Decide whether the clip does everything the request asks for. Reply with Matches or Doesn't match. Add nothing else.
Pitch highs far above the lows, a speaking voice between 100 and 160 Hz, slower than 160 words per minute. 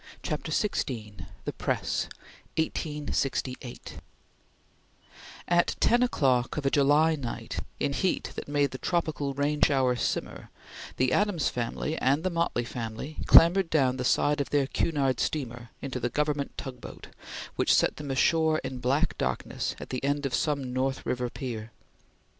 Doesn't match